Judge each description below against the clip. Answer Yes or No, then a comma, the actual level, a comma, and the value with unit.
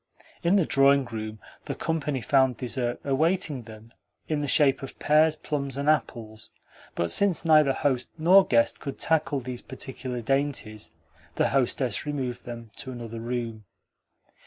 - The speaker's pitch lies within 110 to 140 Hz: Yes, low, 135 Hz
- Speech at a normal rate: Yes, average, 150 wpm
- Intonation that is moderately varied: Yes, average, 3.8 semitones